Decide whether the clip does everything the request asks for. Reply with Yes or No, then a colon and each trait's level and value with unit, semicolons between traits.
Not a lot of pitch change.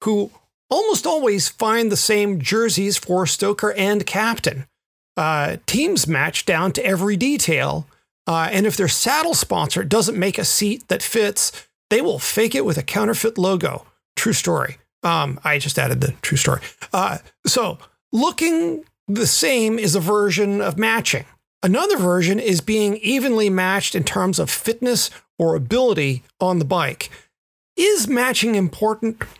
No: average, 3.8 semitones